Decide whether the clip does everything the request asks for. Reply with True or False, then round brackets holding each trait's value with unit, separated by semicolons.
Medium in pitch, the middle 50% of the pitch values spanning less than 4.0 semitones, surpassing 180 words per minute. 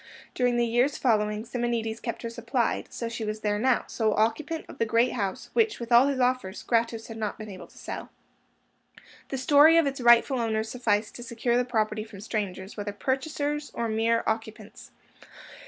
False (230 Hz; 2.5 semitones; 190 wpm)